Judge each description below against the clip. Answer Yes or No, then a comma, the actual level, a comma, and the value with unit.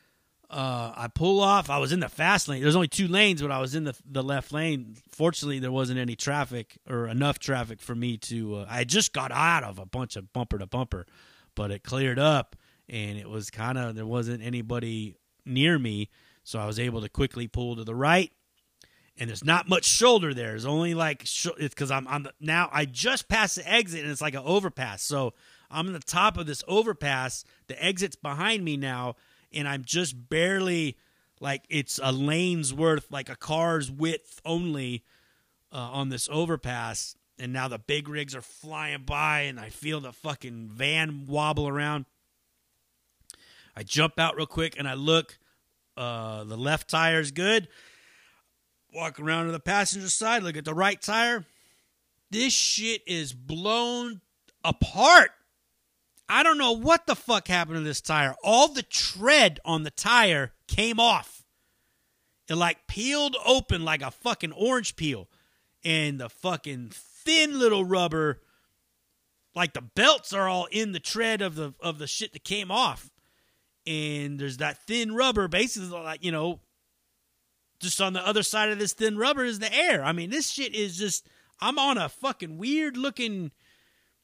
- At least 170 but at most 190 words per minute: Yes, average, 180 wpm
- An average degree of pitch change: No, wide, 6.9 semitones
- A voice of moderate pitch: Yes, medium, 155 Hz